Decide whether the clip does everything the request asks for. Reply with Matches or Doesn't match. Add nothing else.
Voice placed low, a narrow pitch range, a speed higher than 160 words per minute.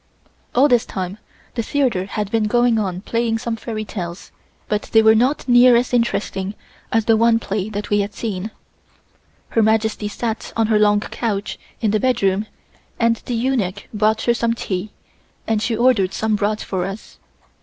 Doesn't match